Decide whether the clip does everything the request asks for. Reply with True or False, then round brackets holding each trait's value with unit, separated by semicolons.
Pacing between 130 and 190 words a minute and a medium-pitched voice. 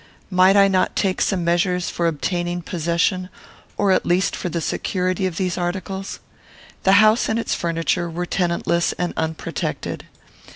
True (155 wpm; 180 Hz)